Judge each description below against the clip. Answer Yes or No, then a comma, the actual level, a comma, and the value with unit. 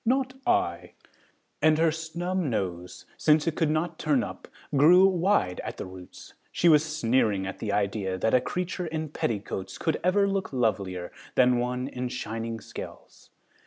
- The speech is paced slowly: No, average, 165 wpm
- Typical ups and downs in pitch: No, wide, 8.2 semitones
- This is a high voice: No, low, 135 Hz